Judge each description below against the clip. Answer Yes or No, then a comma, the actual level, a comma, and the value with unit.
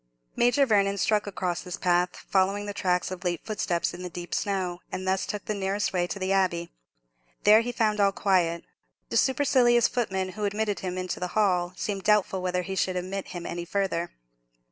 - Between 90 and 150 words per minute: No, average, 200 wpm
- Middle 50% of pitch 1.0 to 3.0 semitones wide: Yes, narrow, 2.4 semitones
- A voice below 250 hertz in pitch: Yes, high, 190 Hz